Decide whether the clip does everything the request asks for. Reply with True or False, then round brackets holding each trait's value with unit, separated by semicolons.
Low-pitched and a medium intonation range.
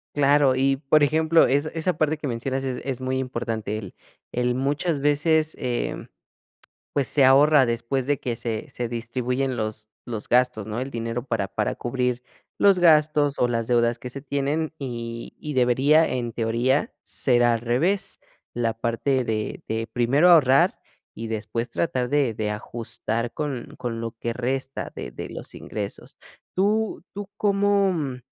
True (130 Hz; 3.8 semitones)